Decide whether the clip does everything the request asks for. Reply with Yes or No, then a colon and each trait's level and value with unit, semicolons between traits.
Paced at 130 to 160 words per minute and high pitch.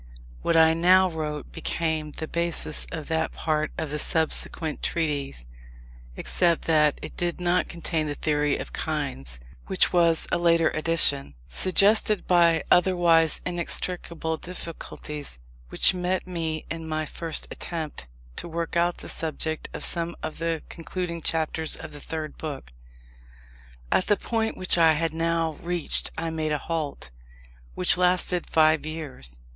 No: average, 145 wpm; medium, 160 Hz